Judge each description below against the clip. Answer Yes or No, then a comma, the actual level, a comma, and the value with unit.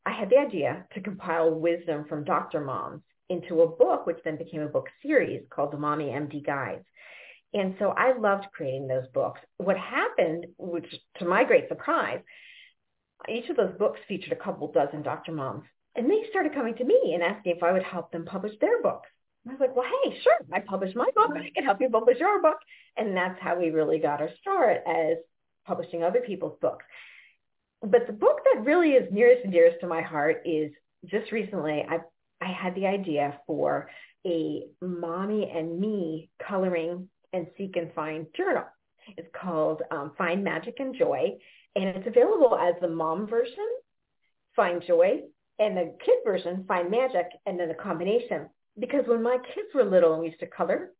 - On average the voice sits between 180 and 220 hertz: Yes, high, 190 Hz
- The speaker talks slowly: No, average, 190 wpm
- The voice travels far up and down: Yes, wide, 8.1 semitones